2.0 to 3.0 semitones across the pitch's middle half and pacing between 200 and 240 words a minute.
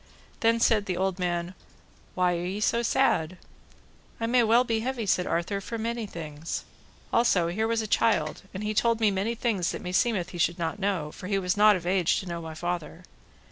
No: average, 4.4 semitones; fast, 205 wpm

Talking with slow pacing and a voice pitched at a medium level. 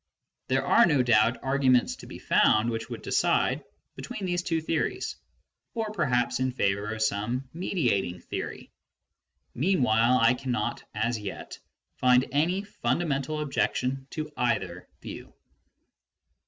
No: slow, 130 wpm; low, 125 Hz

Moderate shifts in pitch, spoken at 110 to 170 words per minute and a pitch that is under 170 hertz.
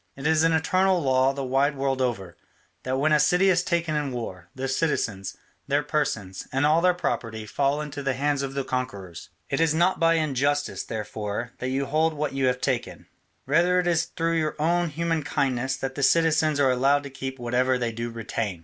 No: average, 3.8 semitones; fast, 205 wpm; medium, 140 Hz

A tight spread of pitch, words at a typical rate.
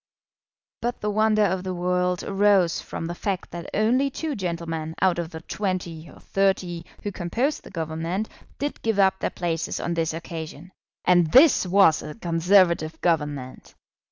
No: average, 3.4 semitones; average, 160 wpm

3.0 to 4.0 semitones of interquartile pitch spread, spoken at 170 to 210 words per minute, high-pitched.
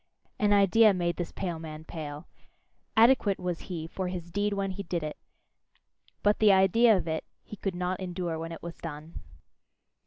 No: average, 3.3 semitones; average, 180 wpm; medium, 180 Hz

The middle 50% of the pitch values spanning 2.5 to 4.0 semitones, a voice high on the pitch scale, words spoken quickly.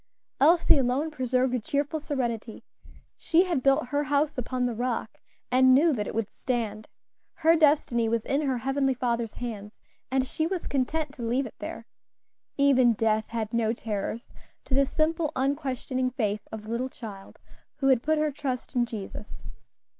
No: average, 3.7 semitones; very high, 255 Hz; average, 170 wpm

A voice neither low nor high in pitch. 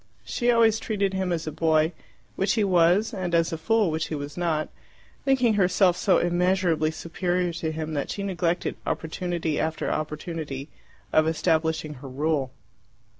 Yes: medium, 170 Hz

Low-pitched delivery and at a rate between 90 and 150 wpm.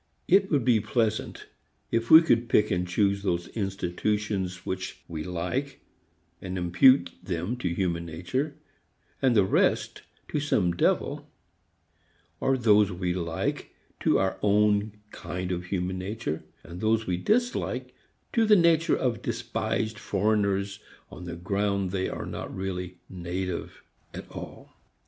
Yes: low, 100 Hz; slow, 135 wpm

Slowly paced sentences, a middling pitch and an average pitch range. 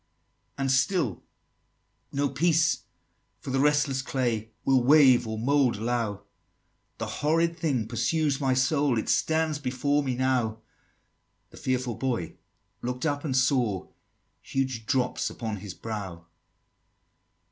No: slow, 125 wpm; low, 130 Hz; average, 3.8 semitones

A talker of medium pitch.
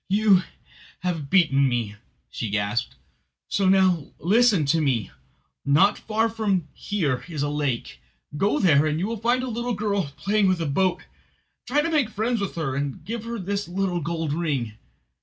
Yes: medium, 180 Hz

